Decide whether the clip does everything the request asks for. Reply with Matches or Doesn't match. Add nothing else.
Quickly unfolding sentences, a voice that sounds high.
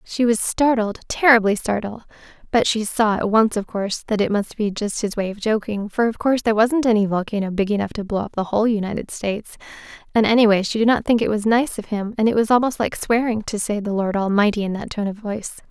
Matches